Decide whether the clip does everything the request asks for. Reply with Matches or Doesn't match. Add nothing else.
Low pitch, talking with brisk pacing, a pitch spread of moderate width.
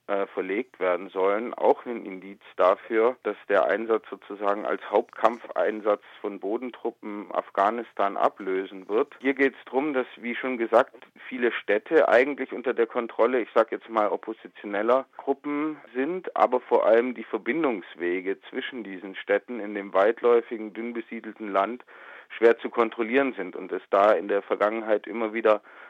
Doesn't match